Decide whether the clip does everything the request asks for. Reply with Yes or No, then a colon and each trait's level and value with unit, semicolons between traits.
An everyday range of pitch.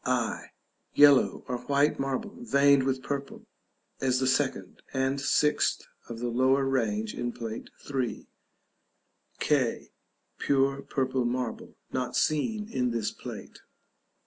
No: narrow, 2.2 semitones